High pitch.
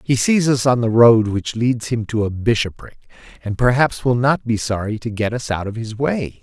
No: low, 115 Hz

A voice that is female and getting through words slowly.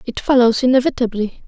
Yes: female; slow, 120 wpm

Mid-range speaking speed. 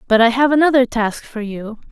No: fast, 220 wpm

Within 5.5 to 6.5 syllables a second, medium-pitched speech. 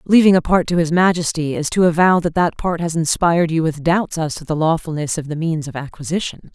Yes: 5.7 syllables/s; medium, 165 Hz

